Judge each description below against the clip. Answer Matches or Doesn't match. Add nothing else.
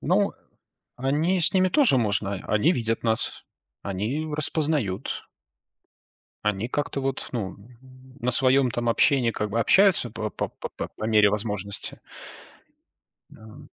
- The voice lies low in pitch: Matches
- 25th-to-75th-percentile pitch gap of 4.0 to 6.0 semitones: Matches